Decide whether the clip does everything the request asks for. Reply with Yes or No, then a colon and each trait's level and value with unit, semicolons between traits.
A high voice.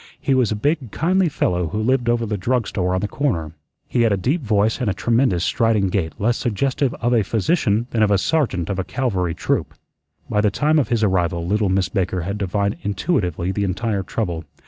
No: low, 105 Hz